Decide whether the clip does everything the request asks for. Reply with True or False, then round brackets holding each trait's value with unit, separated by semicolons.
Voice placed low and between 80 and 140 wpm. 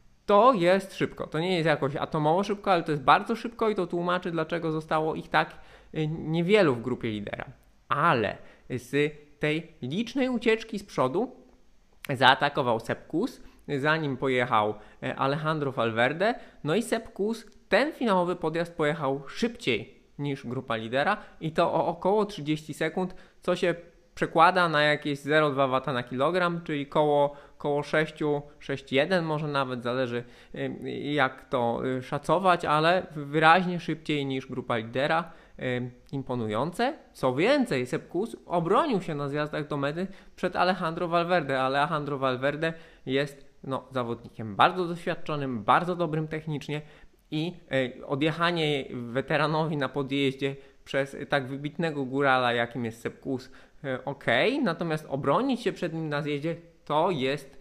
False (150 Hz; 130 wpm)